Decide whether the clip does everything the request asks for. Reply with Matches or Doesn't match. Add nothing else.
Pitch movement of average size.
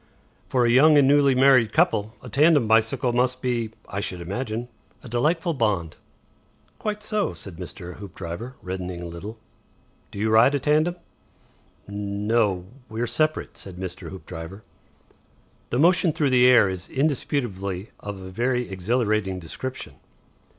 Doesn't match